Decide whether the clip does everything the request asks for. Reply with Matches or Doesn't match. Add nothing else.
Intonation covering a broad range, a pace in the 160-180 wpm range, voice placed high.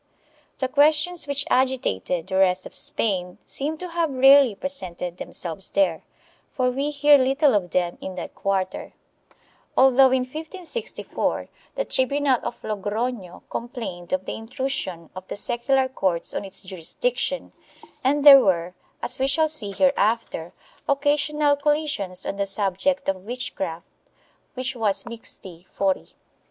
Doesn't match